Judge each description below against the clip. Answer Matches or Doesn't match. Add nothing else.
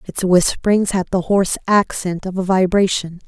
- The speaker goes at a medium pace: Matches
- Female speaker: Matches